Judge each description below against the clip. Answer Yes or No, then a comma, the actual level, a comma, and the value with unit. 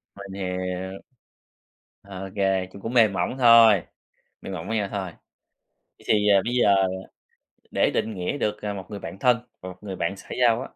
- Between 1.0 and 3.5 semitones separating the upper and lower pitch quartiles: Yes, average, 2.9 semitones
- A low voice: Yes, low, 100 Hz